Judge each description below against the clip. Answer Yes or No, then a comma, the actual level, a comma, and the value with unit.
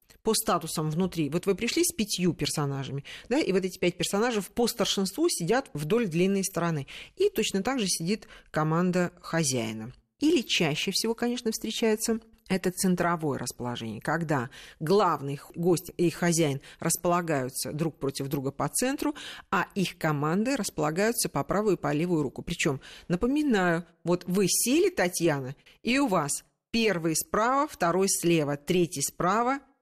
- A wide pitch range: Yes, wide, 5.9 semitones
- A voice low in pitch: No, medium, 175 Hz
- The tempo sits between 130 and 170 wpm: Yes, average, 145 wpm